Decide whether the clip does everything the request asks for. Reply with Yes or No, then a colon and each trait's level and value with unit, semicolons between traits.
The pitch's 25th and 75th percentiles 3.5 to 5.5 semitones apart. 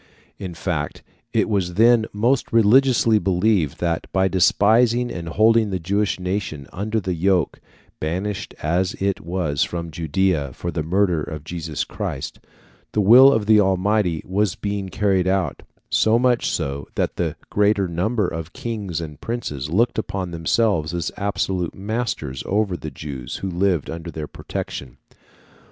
Yes: average, 4.2 semitones